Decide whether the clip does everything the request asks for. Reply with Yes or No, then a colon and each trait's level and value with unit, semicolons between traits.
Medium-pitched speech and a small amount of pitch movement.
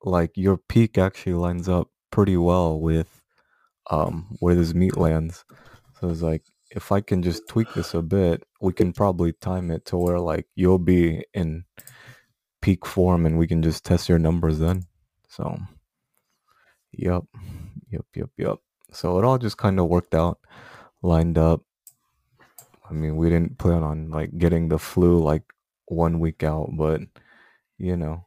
No: very low, 85 Hz; narrow, 2.2 semitones